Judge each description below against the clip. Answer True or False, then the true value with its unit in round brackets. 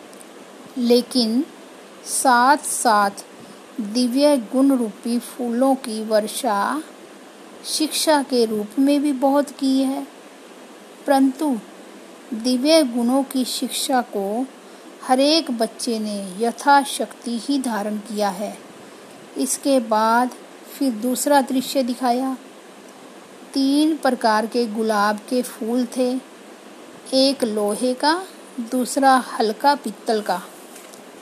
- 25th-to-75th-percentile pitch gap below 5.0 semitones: True (3.1 semitones)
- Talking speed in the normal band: False (100 wpm)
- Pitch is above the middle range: True (255 Hz)